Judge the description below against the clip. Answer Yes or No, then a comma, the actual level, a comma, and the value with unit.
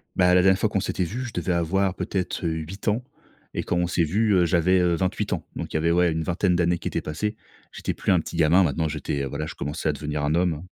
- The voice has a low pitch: Yes, very low, 85 Hz